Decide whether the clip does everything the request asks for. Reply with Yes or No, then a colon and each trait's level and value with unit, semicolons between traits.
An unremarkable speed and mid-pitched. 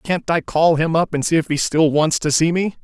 No: fast, 295 wpm; medium, 160 Hz